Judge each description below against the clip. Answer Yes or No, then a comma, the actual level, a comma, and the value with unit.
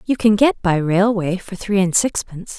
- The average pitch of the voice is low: No, high, 195 Hz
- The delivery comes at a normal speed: No, fast, 210 wpm